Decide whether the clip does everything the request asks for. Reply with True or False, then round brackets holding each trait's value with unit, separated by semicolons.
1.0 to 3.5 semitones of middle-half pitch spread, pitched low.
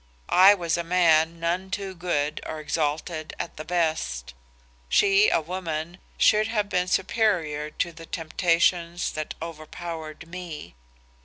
False (2.6 semitones; 170 Hz)